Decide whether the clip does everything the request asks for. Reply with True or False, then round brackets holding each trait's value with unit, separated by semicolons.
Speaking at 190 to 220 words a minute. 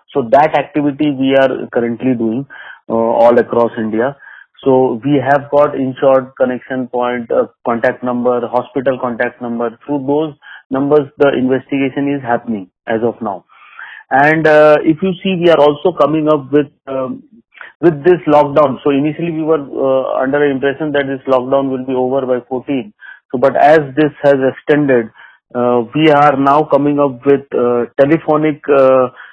False (165 wpm)